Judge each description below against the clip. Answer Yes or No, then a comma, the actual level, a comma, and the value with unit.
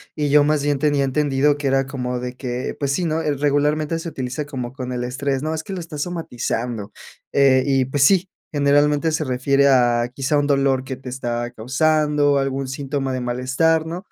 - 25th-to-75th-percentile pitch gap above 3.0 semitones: No, narrow, 2.5 semitones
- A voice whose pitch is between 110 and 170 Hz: Yes, medium, 140 Hz